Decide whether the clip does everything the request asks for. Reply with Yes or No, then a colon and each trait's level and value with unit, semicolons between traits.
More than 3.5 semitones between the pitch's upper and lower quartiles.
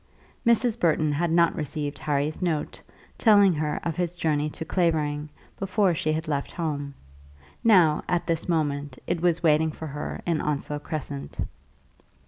No: average, 2.7 semitones